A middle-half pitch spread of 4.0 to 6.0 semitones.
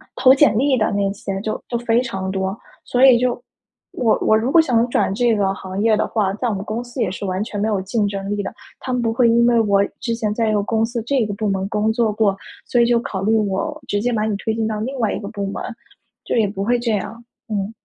No: average, 2.8 semitones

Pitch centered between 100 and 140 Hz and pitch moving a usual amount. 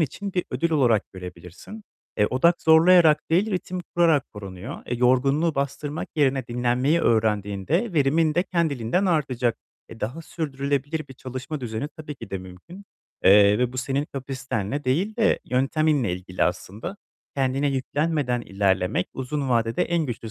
No: low, 135 Hz; wide, 5.8 semitones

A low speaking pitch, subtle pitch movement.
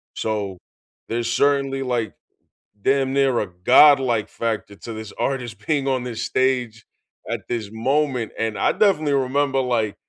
No: low, 125 Hz; average, 3.5 semitones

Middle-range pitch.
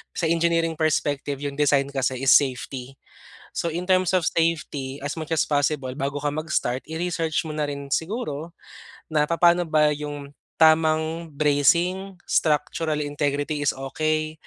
Yes: medium, 150 Hz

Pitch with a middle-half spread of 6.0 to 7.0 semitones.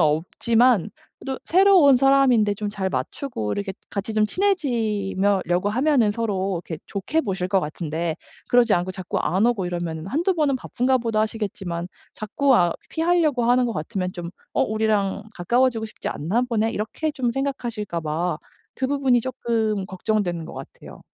No: average, 5.3 semitones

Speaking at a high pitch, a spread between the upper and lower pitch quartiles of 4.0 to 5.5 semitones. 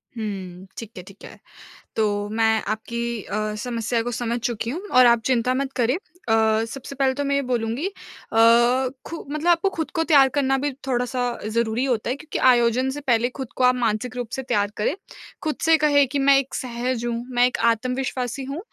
No: high, 245 Hz; average, 2.9 semitones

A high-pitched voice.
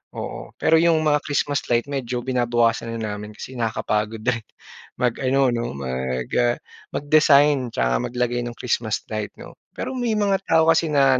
No: low, 125 Hz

